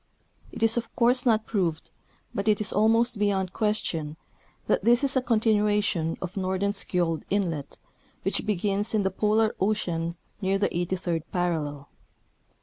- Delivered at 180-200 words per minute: No, average, 145 wpm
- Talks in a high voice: Yes, high, 200 Hz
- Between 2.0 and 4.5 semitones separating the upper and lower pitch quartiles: Yes, average, 3.6 semitones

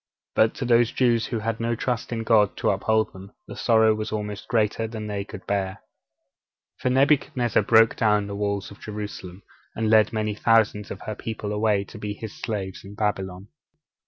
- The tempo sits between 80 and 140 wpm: No, average, 190 wpm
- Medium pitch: No, low, 110 Hz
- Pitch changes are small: Yes, narrow, 1.8 semitones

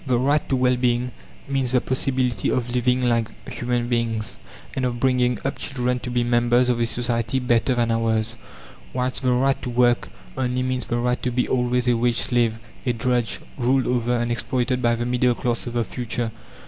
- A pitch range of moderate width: No, narrow, 1.1 semitones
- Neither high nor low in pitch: No, low, 125 Hz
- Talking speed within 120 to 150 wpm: No, average, 200 wpm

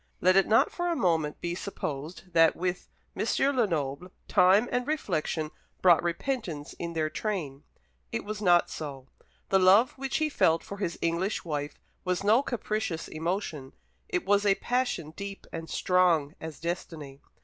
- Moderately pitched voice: Yes, medium, 180 Hz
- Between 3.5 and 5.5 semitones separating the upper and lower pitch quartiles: Yes, average, 4.4 semitones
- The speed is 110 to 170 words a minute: Yes, average, 160 wpm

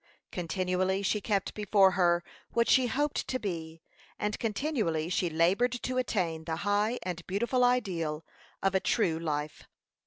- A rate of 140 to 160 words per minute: Yes, average, 150 wpm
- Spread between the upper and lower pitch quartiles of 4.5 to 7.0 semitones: Yes, average, 5.2 semitones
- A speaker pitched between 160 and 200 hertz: Yes, high, 190 Hz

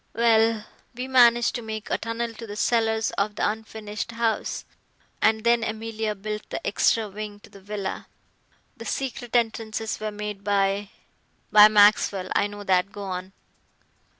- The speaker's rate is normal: Yes, average, 160 wpm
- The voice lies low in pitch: No, high, 215 Hz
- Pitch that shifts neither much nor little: No, narrow, 1.7 semitones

